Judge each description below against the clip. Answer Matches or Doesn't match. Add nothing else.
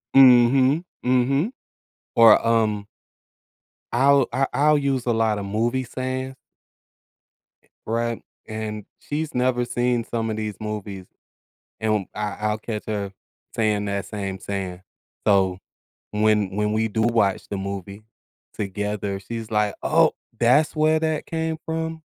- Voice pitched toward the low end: Matches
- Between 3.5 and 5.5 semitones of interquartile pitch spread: Matches